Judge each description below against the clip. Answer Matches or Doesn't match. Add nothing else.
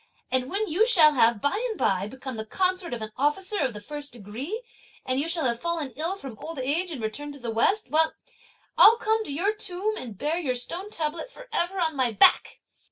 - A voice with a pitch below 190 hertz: Doesn't match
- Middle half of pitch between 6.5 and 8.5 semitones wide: Matches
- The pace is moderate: Doesn't match